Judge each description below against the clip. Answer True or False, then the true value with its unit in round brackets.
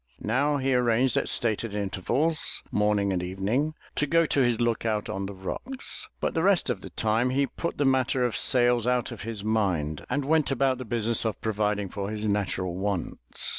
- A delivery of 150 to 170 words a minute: False (200 wpm)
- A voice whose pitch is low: True (115 Hz)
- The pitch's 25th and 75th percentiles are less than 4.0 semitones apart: False (4.4 semitones)